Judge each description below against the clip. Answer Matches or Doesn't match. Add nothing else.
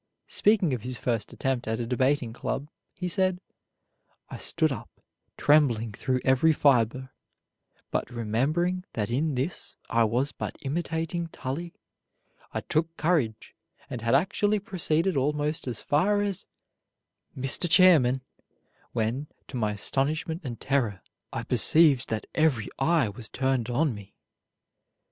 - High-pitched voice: Doesn't match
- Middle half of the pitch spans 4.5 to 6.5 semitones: Matches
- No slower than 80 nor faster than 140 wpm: Matches